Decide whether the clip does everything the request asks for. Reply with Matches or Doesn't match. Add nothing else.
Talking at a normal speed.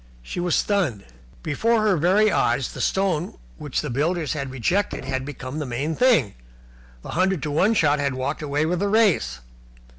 Matches